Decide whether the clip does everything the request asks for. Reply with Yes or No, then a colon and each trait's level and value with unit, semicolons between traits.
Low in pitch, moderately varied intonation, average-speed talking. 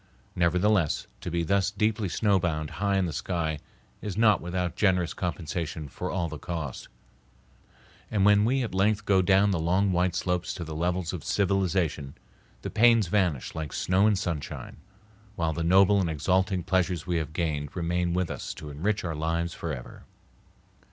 Yes: very low, 90 Hz; average, 3.0 semitones; average, 170 wpm